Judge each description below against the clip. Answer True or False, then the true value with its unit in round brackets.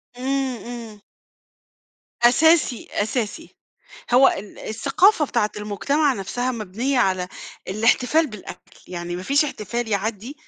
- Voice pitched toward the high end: True (240 Hz)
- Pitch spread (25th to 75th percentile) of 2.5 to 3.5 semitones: False (4.8 semitones)